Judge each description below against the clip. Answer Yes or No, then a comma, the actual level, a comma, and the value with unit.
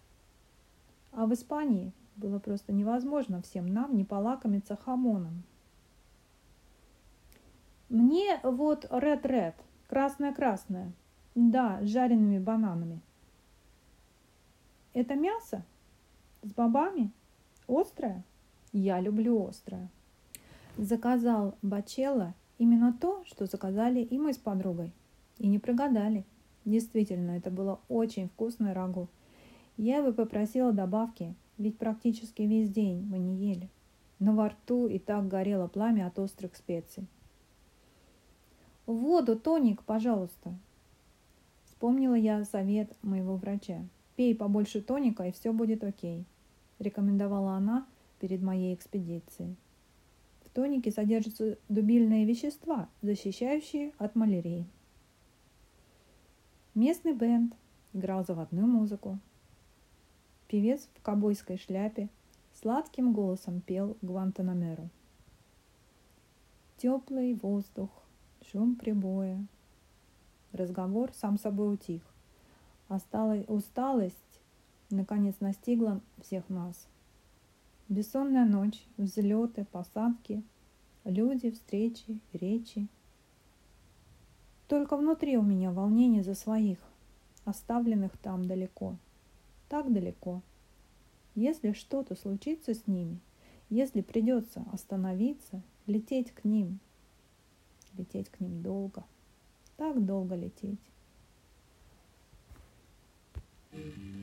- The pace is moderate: No, slow, 90 wpm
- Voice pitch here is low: No, high, 210 Hz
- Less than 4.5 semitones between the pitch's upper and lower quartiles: Yes, average, 3.7 semitones